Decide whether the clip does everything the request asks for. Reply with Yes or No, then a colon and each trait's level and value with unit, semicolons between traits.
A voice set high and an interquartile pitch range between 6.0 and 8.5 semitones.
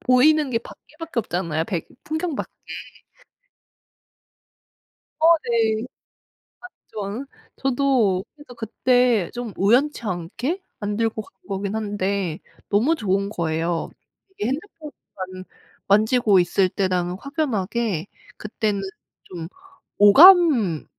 No: high, 215 Hz; wide, 5.5 semitones